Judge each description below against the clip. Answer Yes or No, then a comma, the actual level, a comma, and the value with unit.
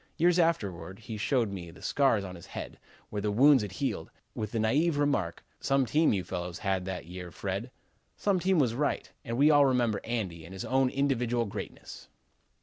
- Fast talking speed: No, average, 195 wpm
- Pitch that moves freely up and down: Yes, wide, 6.5 semitones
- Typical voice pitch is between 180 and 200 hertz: No, low, 115 Hz